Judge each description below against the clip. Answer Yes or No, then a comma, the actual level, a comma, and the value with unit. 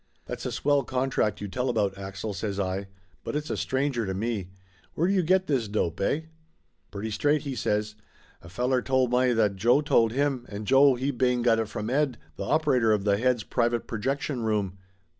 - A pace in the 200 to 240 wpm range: Yes, fast, 205 wpm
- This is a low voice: Yes, low, 120 Hz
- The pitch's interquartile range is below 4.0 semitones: No, average, 4.3 semitones